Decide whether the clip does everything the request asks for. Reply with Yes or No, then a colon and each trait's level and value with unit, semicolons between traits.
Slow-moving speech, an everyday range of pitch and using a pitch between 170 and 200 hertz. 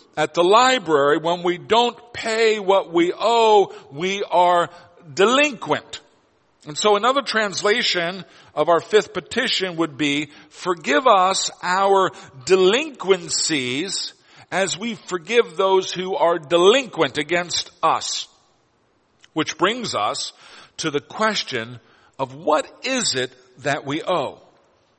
Yes: slow, 120 wpm; average, 5.0 semitones; medium, 185 Hz